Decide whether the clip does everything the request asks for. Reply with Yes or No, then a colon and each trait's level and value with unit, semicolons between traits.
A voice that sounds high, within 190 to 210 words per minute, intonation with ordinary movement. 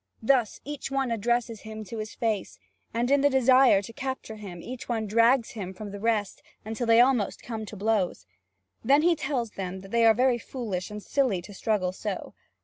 Yes: high, 225 Hz; average, 200 wpm; average, 3.6 semitones